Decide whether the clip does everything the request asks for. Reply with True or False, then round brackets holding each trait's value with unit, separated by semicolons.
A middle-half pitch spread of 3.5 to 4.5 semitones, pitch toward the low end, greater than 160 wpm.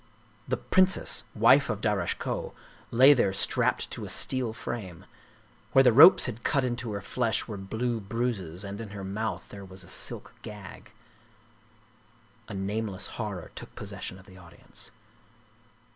False (3.8 semitones; 105 Hz; 155 wpm)